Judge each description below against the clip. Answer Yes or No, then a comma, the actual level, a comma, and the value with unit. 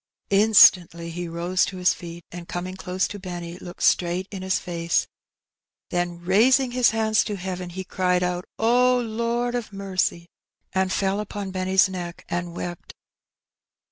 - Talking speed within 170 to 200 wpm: No, average, 155 wpm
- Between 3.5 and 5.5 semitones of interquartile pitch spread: No, average, 2.7 semitones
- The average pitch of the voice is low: No, medium, 185 Hz